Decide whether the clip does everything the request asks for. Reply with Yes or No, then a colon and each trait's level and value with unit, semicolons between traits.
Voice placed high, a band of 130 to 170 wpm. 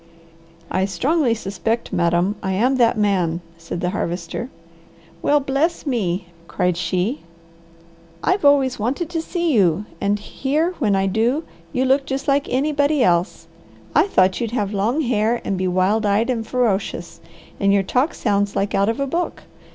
Yes: high, 220 Hz; average, 165 wpm